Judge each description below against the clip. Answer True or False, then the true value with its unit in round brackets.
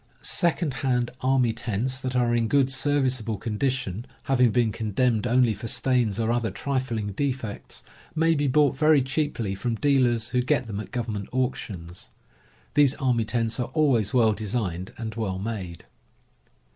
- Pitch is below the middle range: True (120 Hz)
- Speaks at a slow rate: False (160 wpm)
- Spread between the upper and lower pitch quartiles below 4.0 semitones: True (3.2 semitones)